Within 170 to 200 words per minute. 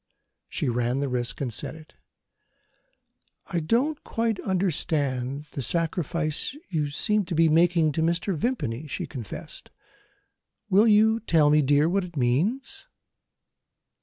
No: slow, 135 wpm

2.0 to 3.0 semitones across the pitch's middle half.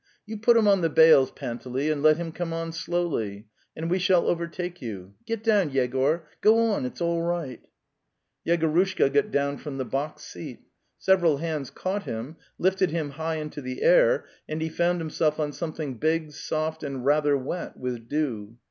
No: average, 3.8 semitones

